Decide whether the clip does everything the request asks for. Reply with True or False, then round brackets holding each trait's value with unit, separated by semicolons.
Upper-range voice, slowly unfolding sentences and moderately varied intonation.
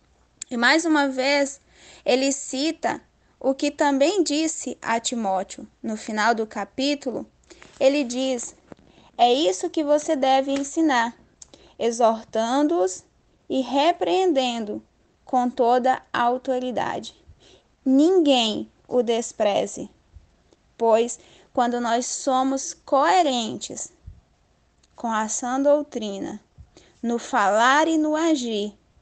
True (260 Hz; 95 wpm; 3.8 semitones)